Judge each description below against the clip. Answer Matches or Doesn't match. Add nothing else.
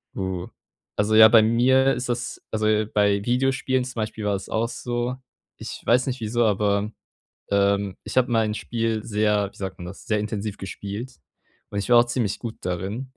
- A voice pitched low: Matches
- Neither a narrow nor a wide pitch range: Matches